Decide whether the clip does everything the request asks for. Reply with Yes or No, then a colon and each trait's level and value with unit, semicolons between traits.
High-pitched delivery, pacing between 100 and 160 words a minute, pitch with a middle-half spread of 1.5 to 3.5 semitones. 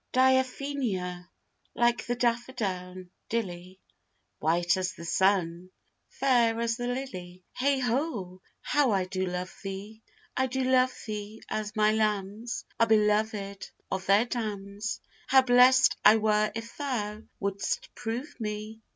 No: high, 215 Hz; slow, 135 wpm; average, 4.3 semitones